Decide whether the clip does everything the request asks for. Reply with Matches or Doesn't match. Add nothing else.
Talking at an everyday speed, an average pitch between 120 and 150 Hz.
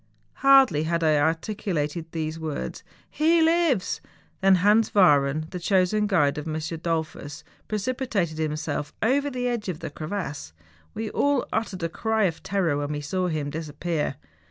Doesn't match